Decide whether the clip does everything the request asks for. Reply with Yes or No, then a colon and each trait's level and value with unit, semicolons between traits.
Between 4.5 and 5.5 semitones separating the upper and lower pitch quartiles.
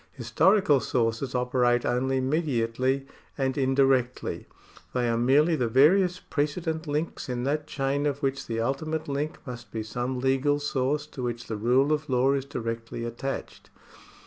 No: average, 3.0 semitones